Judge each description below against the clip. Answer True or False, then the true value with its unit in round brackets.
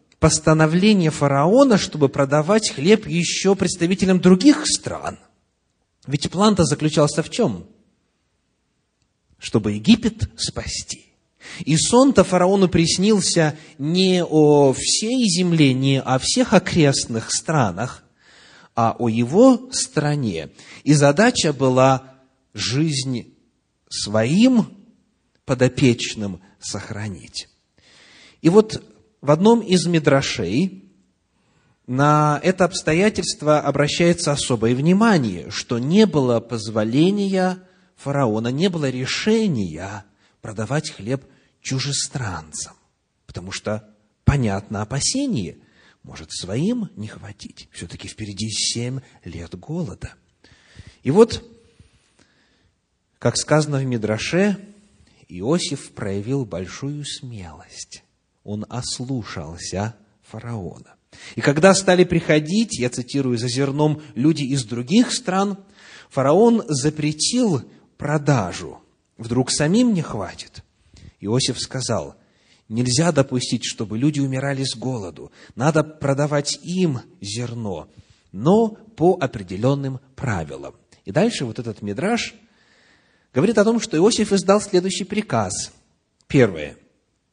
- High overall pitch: False (140 Hz)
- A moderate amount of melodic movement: False (7.7 semitones)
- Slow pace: True (95 wpm)